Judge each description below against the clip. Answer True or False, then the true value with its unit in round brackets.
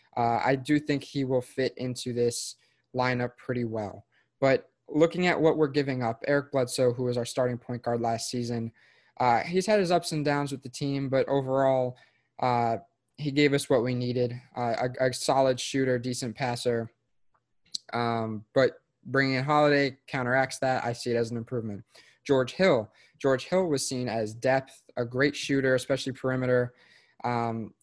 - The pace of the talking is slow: False (175 wpm)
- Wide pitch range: False (2.4 semitones)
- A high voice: False (130 Hz)